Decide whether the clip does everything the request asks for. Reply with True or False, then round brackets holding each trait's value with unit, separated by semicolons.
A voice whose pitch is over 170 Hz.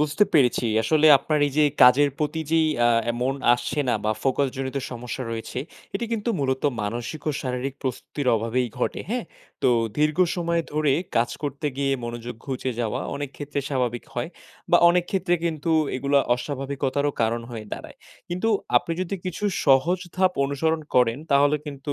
False (140 Hz)